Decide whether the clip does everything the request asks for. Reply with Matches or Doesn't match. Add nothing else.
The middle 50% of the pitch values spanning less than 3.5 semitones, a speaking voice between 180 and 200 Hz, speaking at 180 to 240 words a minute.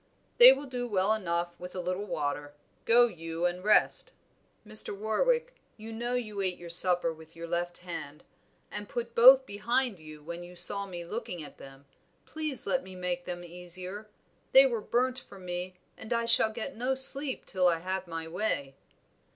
Doesn't match